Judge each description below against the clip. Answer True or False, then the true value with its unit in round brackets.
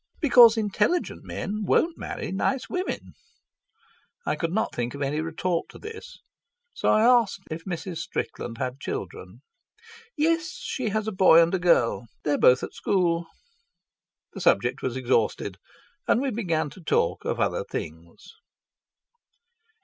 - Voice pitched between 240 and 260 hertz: False (185 Hz)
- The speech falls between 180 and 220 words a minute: False (145 wpm)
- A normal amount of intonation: False (7.9 semitones)